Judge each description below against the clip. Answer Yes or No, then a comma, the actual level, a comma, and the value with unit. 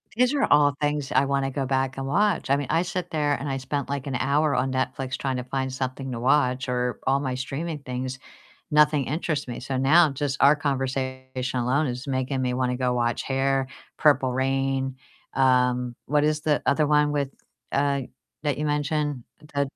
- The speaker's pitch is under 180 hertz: Yes, low, 135 Hz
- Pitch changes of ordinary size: No, narrow, 2.1 semitones